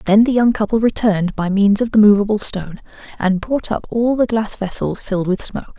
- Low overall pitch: No, high, 210 Hz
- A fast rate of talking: Yes, fast, 220 wpm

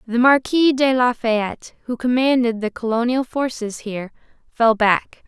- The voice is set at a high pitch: Yes, high, 240 Hz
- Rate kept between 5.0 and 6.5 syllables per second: No, 4.5 syllables/s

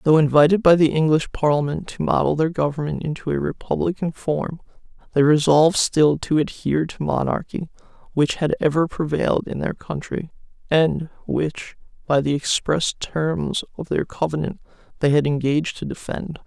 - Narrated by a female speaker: No, male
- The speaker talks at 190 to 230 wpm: No, average, 155 wpm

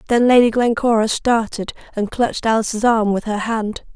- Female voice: Yes, female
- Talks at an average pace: Yes, average, 165 wpm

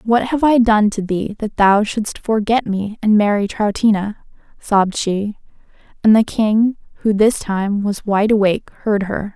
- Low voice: No, high, 210 Hz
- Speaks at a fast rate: No, average, 175 wpm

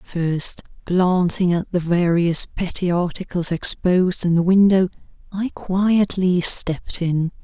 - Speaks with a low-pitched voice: No, medium, 180 Hz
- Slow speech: Yes, slow, 120 wpm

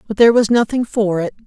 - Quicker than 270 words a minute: No, fast, 245 wpm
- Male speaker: No, female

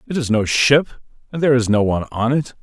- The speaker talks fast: Yes, fast, 250 wpm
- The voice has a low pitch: Yes, low, 125 Hz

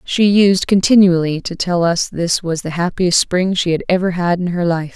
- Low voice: No, medium, 175 Hz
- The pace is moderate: No, fast, 220 wpm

